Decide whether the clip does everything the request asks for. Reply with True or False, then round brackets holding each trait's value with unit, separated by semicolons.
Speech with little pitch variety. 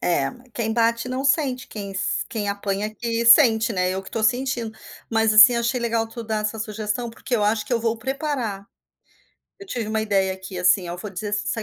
True (2.3 semitones)